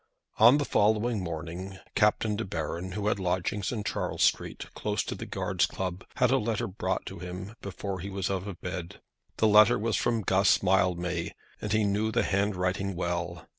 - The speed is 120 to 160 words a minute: No, average, 185 wpm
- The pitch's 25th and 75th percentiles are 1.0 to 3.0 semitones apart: Yes, average, 2.7 semitones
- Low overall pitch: Yes, very low, 95 Hz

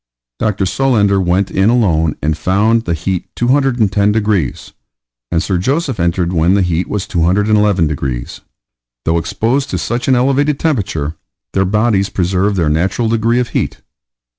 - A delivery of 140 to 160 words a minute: Yes, average, 150 wpm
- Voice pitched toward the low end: Yes, low, 100 Hz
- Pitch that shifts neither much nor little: Yes, average, 4.9 semitones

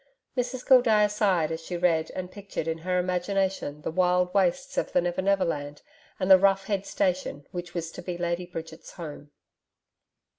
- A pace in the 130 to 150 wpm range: No, average, 180 wpm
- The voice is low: No, medium, 180 Hz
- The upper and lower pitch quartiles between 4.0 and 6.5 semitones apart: No, average, 2.8 semitones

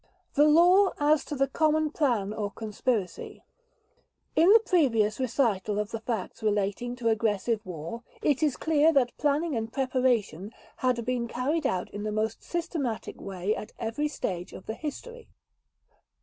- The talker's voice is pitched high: Yes, high, 245 Hz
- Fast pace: No, average, 155 wpm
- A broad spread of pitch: Yes, wide, 5.8 semitones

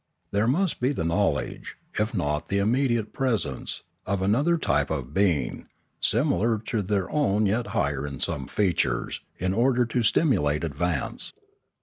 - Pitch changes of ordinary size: No, wide, 6.7 semitones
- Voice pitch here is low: Yes, low, 100 Hz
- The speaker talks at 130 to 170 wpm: Yes, average, 145 wpm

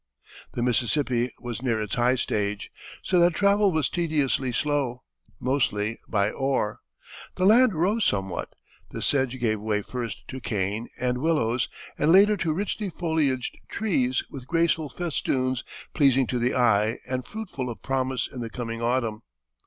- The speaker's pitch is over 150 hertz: No, low, 130 Hz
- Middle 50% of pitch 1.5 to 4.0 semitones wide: No, average, 5.2 semitones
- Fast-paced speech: No, average, 155 wpm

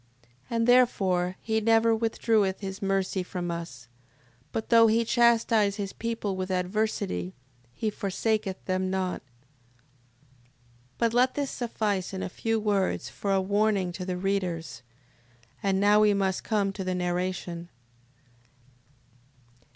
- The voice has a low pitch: No, high, 195 Hz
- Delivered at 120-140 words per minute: Yes, slow, 135 wpm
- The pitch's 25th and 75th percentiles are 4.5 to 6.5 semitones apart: No, average, 3.0 semitones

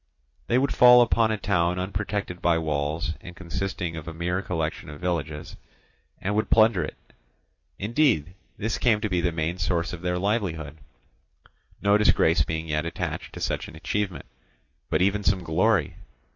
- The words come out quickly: No, average, 165 wpm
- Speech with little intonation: No, average, 4.1 semitones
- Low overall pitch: Yes, very low, 90 Hz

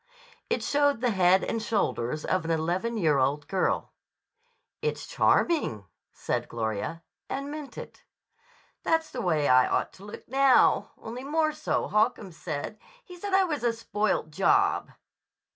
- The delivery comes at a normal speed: Yes, average, 150 wpm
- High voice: Yes, high, 215 Hz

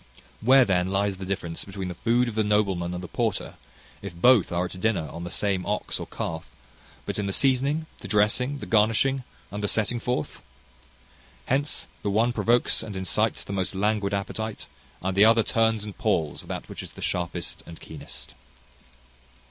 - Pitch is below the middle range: Yes, low, 105 Hz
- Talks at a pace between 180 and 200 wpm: Yes, average, 185 wpm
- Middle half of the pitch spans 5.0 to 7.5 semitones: No, average, 3.3 semitones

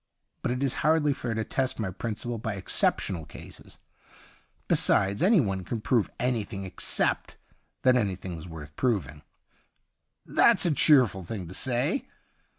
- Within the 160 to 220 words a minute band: No, average, 150 wpm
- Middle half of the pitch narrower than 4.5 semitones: No, average, 5.3 semitones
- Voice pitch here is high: No, low, 110 Hz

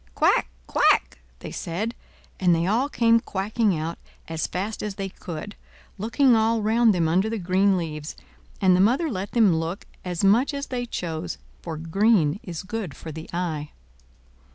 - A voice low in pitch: No, high, 195 Hz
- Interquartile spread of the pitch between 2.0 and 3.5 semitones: No, average, 5.1 semitones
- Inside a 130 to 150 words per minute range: No, average, 170 wpm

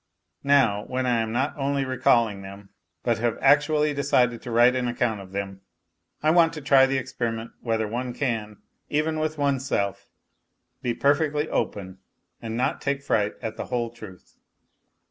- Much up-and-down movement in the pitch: No, average, 4.1 semitones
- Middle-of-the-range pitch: No, low, 125 Hz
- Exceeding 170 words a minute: No, average, 165 wpm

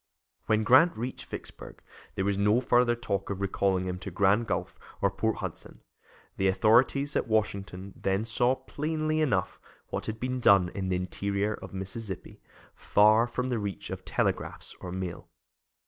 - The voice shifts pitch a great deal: No, average, 3.9 semitones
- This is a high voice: No, low, 105 Hz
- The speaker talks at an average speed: Yes, average, 165 wpm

